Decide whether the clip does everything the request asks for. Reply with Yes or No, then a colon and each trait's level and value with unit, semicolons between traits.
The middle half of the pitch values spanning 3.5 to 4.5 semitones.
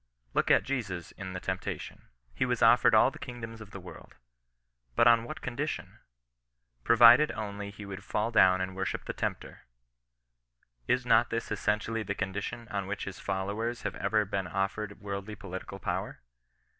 No: average, 2.8 semitones